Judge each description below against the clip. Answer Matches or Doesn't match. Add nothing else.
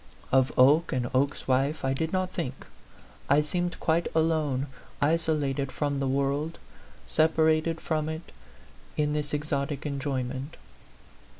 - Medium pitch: Matches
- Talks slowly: Matches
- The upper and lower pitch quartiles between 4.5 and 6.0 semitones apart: Doesn't match